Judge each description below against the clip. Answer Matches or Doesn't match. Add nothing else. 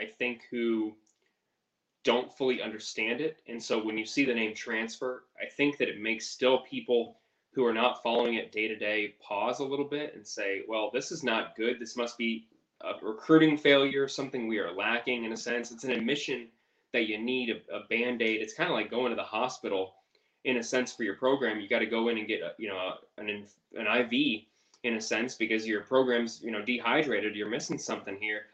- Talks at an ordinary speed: Doesn't match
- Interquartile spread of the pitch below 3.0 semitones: Matches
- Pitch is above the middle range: Doesn't match